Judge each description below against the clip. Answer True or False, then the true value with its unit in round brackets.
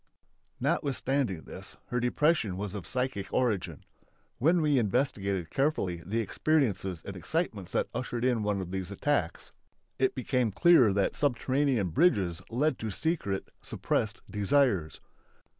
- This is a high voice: False (115 Hz)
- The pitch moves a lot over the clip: True (5.9 semitones)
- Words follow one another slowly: True (130 wpm)